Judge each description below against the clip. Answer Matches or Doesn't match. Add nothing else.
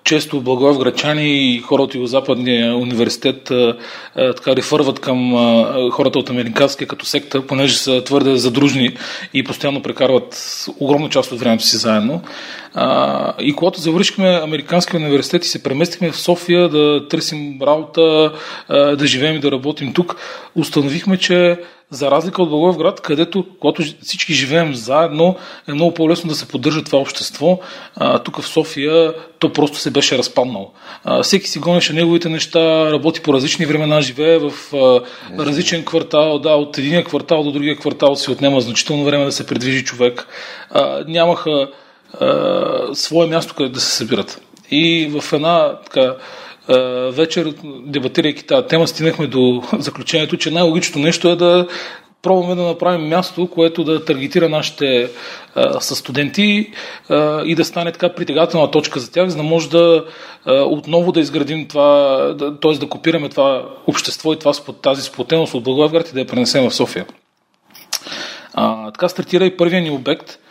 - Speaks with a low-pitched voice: Doesn't match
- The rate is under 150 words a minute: Doesn't match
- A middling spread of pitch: Matches